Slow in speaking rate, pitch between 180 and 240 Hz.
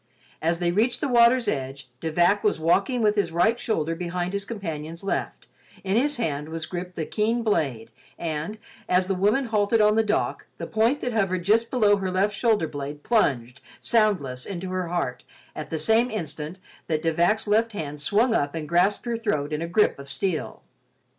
No: average, 195 wpm; medium, 185 Hz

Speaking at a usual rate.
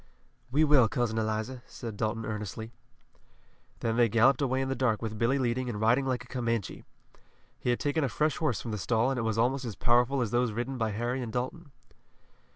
No: fast, 210 wpm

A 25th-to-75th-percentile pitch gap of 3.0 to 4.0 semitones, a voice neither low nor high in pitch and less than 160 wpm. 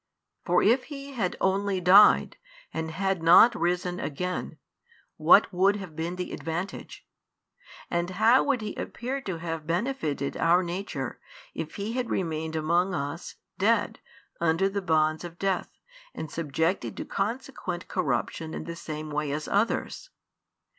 Yes: average, 3.7 semitones; medium, 180 Hz; average, 145 wpm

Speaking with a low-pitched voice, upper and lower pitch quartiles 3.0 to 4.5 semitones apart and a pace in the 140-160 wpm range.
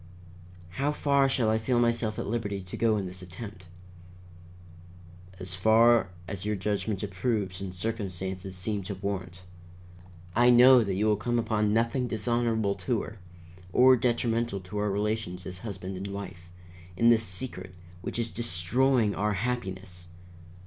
Yes: low, 105 Hz; average, 3.9 semitones; average, 150 wpm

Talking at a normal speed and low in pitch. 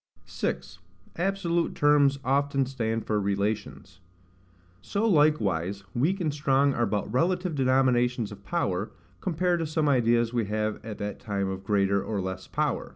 Yes: average, 150 wpm; low, 120 Hz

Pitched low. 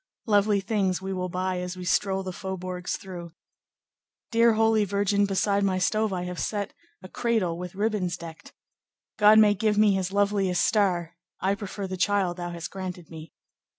No: high, 190 Hz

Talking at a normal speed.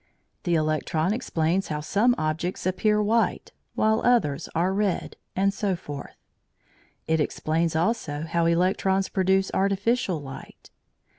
No: slow, 125 wpm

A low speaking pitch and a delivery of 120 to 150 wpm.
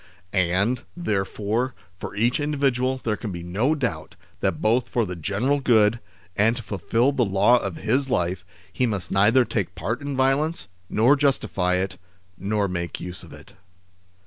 No: low, 110 Hz; average, 165 wpm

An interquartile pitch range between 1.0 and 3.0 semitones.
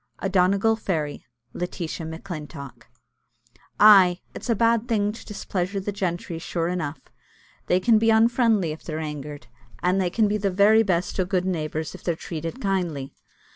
No: average, 4.0 semitones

